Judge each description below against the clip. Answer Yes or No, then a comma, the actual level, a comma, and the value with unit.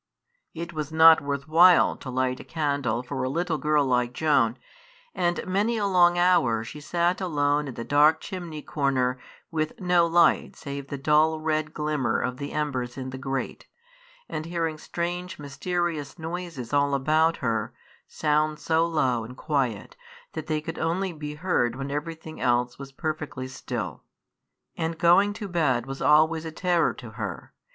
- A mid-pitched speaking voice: Yes, medium, 150 Hz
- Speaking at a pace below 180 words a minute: Yes, average, 165 wpm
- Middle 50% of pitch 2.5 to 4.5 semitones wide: Yes, average, 3.8 semitones